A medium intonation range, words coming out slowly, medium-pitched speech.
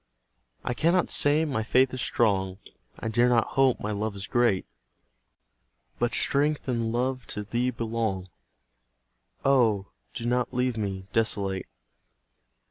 No: average, 3.4 semitones; slow, 130 wpm; low, 115 Hz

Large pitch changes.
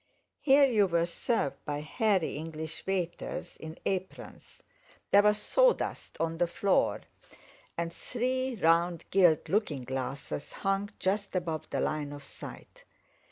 No: average, 4.4 semitones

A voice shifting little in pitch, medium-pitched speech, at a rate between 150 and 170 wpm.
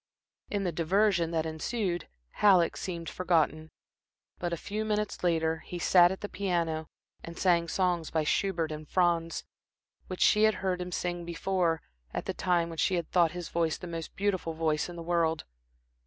No: narrow, 2.1 semitones; medium, 175 Hz; average, 180 wpm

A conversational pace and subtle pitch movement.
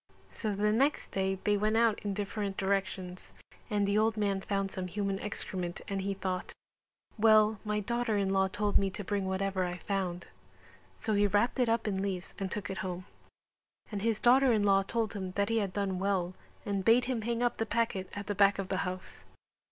No: fast, 210 wpm; narrow, 2.0 semitones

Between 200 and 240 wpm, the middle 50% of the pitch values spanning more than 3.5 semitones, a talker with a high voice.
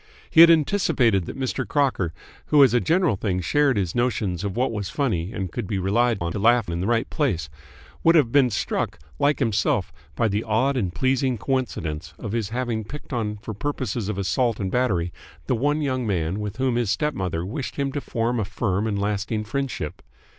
No: fast, 205 wpm; average, 5.0 semitones; low, 115 Hz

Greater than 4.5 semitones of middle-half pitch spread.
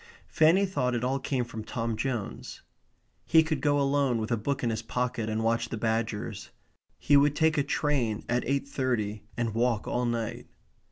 No: average, 3.8 semitones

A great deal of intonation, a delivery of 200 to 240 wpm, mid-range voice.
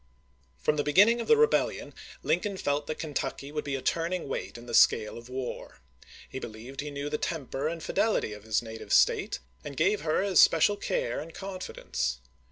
Yes: wide, 6.1 semitones; fast, 205 wpm; medium, 150 Hz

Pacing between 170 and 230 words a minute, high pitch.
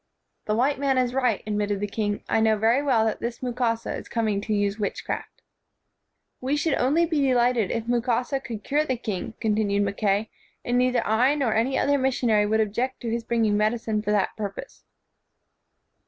Yes: average, 185 wpm; high, 230 Hz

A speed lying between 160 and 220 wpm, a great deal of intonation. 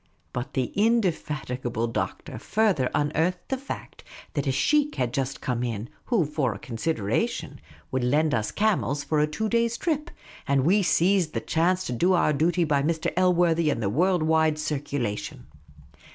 Yes: average, 170 wpm; wide, 5.9 semitones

